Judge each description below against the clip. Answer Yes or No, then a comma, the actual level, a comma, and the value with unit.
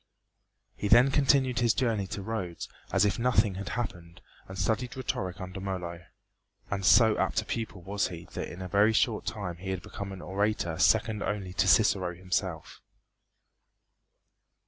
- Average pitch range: Yes, average, 3.4 semitones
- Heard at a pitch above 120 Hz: No, low, 100 Hz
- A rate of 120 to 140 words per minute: No, average, 160 wpm